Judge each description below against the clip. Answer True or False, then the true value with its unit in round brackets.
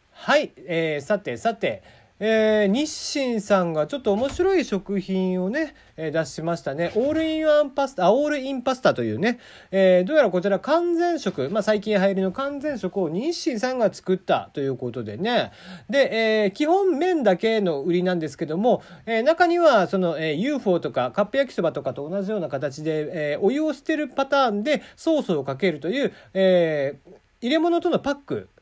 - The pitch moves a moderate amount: False (8.3 semitones)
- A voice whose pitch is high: True (210 Hz)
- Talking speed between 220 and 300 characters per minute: False (340 characters per minute)